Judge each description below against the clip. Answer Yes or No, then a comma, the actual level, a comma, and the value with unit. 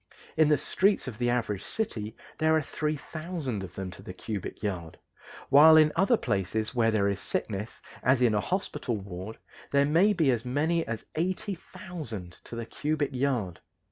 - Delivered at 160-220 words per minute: Yes, average, 175 wpm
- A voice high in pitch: No, low, 125 Hz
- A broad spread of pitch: Yes, wide, 7.0 semitones